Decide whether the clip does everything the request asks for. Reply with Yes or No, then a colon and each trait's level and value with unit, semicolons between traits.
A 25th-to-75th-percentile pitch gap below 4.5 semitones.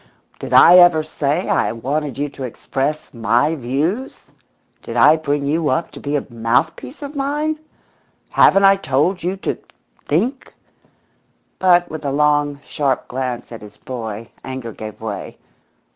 No: average, 5.3 semitones